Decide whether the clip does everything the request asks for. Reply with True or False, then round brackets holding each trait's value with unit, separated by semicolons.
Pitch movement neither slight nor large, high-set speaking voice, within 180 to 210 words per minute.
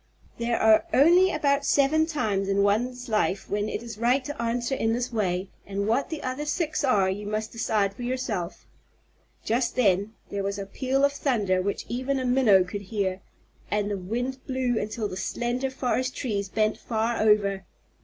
True (4.3 semitones; 225 Hz; 185 wpm)